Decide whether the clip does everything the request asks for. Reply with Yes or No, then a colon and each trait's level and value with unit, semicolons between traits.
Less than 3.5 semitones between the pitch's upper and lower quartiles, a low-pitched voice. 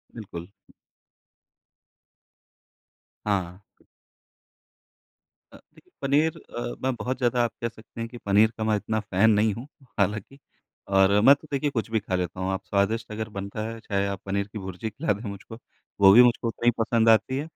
Yes: average, 3.1 semitones; low, 110 Hz